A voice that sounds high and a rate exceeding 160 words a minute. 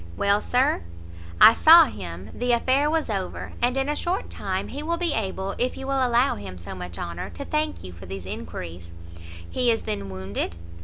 Yes: high, 225 Hz; average, 200 wpm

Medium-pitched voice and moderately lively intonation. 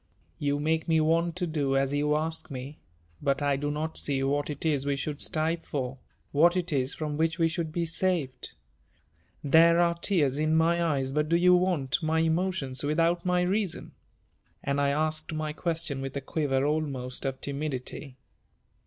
Yes: medium, 155 Hz; average, 3.0 semitones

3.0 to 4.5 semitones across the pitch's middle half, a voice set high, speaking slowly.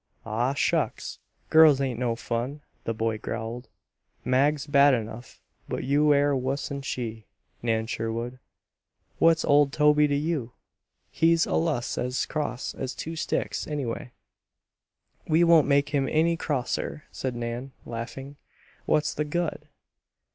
No: average, 3.8 semitones; medium, 140 Hz; slow, 130 wpm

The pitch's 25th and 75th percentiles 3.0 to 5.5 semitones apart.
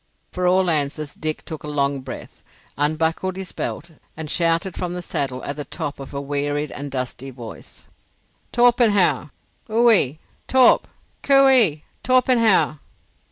Yes: average, 5.1 semitones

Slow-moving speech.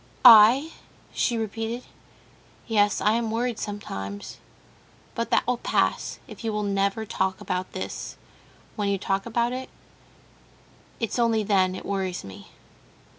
Yes: slow, 130 wpm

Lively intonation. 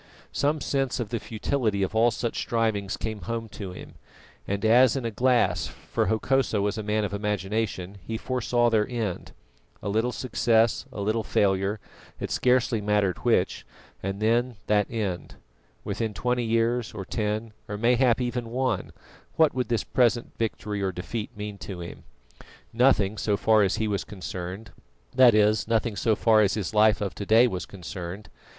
No: narrow, 2.6 semitones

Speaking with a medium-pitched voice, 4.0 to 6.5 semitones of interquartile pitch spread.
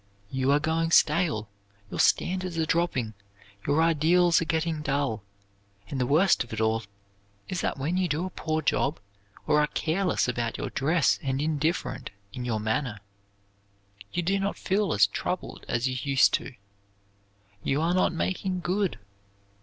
Yes: medium, 155 Hz; average, 4.7 semitones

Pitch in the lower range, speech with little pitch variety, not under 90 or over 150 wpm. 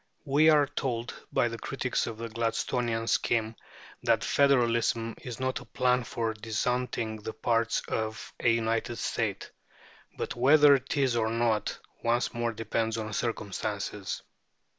Yes: low, 115 Hz; narrow, 2.0 semitones; average, 140 wpm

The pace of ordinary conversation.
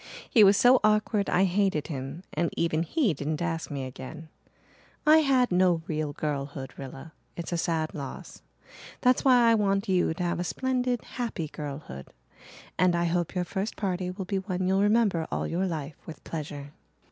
Yes: average, 180 wpm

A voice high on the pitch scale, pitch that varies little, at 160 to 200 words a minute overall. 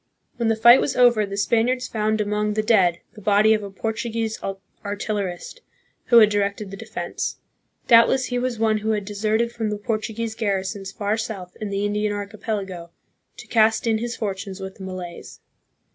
Yes: high, 215 Hz; narrow, 1.9 semitones; average, 180 wpm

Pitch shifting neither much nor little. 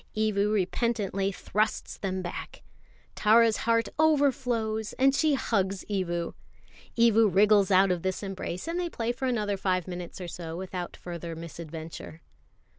Yes: average, 4.1 semitones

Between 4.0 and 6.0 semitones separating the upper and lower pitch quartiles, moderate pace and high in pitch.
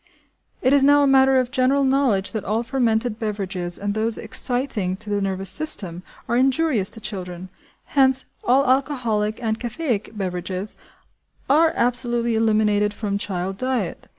Yes: average, 4.7 semitones; average, 150 wpm; high, 225 Hz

